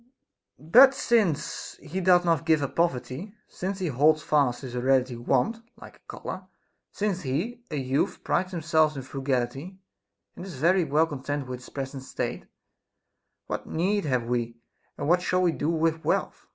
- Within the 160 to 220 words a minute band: Yes, average, 165 wpm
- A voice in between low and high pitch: Yes, medium, 155 Hz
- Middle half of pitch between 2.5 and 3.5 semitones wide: No, average, 5.2 semitones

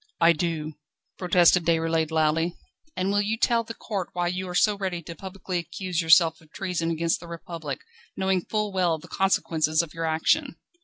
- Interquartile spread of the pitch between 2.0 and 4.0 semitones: Yes, average, 2.7 semitones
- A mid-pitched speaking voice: Yes, medium, 175 Hz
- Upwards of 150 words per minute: Yes, average, 190 wpm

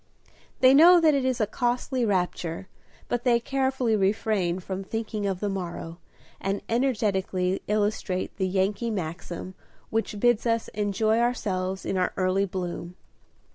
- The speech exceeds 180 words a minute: No, average, 140 wpm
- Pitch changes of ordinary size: Yes, average, 4.1 semitones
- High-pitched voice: Yes, high, 205 Hz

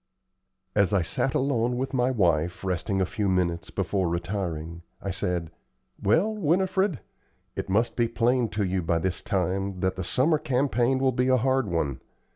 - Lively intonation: Yes, wide, 6.2 semitones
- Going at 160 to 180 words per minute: Yes, average, 170 wpm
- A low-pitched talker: Yes, low, 100 Hz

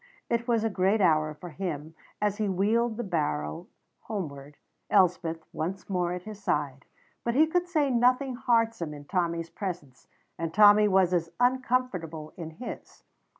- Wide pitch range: Yes, wide, 5.9 semitones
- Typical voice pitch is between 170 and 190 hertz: Yes, medium, 185 Hz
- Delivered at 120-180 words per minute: Yes, average, 155 wpm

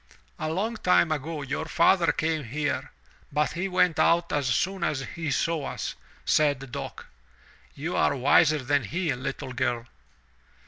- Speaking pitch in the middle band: Yes, medium, 150 Hz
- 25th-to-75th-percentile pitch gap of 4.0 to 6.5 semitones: No, average, 3.5 semitones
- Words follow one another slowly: No, average, 150 wpm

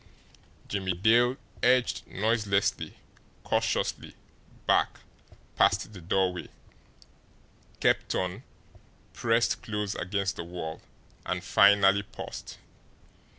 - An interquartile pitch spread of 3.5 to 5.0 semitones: No, average, 3.0 semitones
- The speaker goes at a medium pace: No, slow, 85 wpm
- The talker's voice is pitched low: Yes, low, 100 Hz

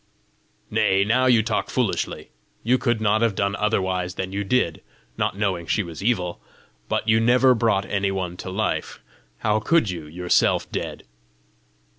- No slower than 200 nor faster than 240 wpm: No, average, 160 wpm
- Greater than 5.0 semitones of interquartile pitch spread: No, average, 3.5 semitones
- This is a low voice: Yes, low, 100 Hz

